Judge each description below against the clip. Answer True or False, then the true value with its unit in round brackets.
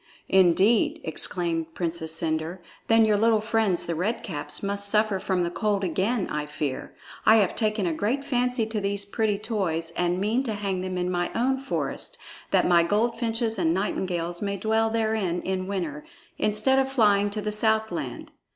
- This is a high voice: True (200 Hz)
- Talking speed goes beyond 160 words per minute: True (180 wpm)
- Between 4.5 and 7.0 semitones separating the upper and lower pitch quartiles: False (4.0 semitones)